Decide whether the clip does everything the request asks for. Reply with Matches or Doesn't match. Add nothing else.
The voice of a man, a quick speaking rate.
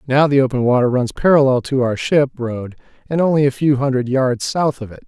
Matches